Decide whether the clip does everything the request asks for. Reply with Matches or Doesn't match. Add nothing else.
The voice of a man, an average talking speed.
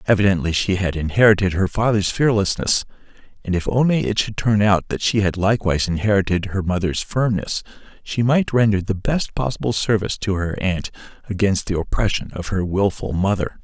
Matches